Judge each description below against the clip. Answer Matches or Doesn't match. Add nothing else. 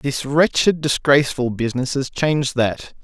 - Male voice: Matches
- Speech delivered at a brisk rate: Doesn't match